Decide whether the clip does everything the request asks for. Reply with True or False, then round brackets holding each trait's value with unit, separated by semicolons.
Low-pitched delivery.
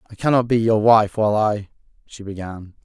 True (110 Hz)